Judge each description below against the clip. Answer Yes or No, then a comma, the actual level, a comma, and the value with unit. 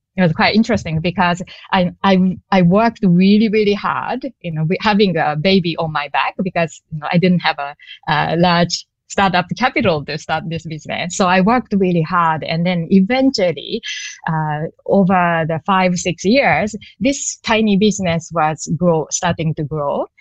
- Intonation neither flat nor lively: Yes, average, 4.1 semitones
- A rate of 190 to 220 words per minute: No, average, 170 wpm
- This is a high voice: No, medium, 180 Hz